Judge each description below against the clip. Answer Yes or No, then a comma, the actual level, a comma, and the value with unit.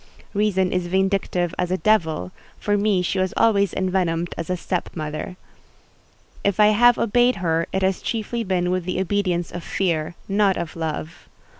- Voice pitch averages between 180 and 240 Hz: Yes, medium, 185 Hz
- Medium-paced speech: Yes, average, 170 wpm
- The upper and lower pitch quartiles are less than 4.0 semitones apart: Yes, narrow, 2.6 semitones